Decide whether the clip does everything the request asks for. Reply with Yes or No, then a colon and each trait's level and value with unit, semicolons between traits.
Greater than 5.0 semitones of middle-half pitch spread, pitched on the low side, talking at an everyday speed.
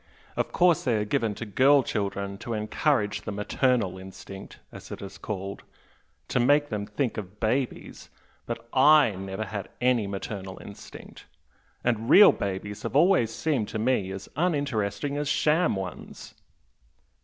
Yes: wide, 5.6 semitones; low, 110 Hz; average, 150 wpm